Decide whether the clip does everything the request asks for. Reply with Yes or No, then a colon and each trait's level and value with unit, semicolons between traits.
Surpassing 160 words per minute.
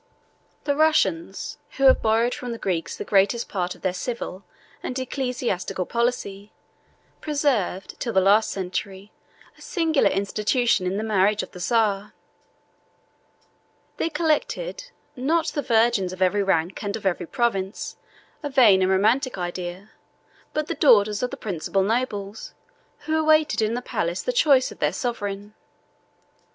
No: average, 145 wpm